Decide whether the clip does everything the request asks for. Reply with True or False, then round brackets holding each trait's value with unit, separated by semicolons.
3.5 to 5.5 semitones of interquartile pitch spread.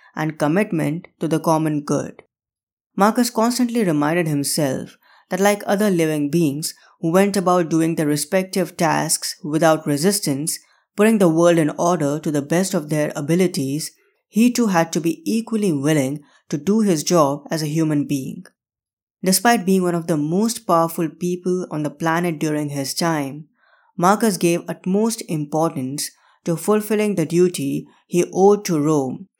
True (3.8 semitones)